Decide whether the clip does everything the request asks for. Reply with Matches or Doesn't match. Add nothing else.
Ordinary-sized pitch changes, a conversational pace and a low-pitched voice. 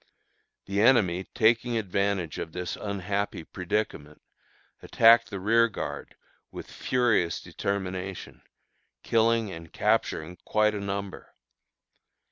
Doesn't match